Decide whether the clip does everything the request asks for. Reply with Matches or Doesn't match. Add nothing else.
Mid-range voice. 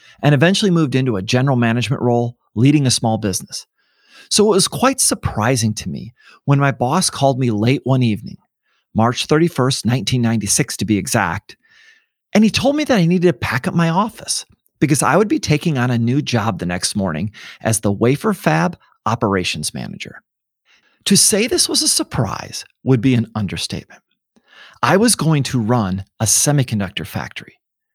Doesn't match